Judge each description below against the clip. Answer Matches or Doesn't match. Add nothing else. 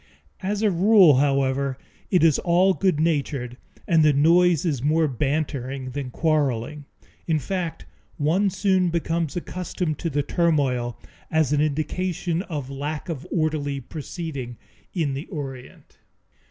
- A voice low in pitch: Doesn't match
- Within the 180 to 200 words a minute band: Doesn't match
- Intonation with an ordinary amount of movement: Matches